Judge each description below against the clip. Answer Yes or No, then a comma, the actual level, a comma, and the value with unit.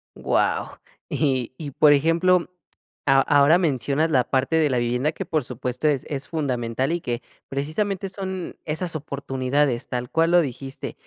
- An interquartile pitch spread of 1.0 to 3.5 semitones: No, average, 4.0 semitones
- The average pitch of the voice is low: No, medium, 145 Hz